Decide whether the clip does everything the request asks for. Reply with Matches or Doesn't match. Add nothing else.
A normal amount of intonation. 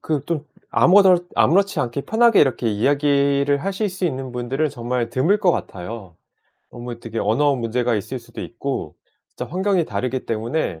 Doesn't match